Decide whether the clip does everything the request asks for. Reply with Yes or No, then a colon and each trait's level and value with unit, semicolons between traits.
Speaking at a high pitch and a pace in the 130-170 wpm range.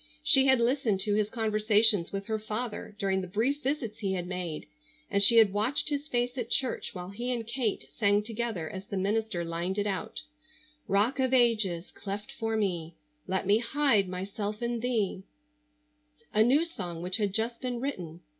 No: high, 215 Hz; average, 185 wpm